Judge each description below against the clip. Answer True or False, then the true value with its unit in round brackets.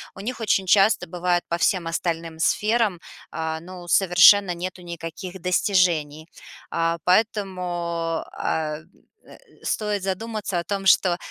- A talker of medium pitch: True (180 Hz)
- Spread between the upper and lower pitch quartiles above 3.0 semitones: False (2.6 semitones)